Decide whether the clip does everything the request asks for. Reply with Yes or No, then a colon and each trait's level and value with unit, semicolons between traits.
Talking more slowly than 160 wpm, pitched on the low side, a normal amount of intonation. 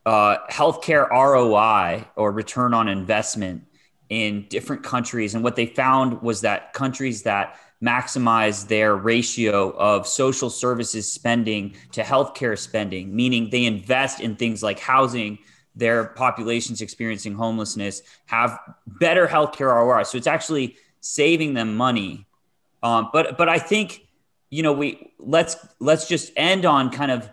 Yes: average, 140 wpm; low, 120 Hz; average, 3.5 semitones